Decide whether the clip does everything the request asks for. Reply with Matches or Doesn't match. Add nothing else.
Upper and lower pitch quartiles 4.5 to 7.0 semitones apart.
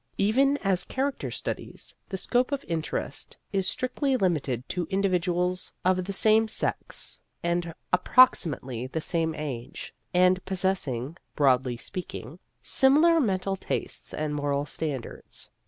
Matches